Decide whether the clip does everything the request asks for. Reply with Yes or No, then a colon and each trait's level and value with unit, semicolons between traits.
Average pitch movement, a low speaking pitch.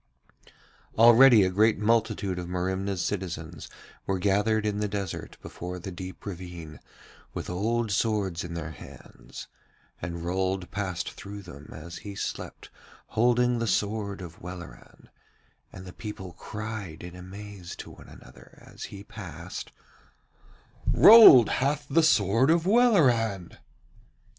Yes: average, 3.9 semitones; low, 100 Hz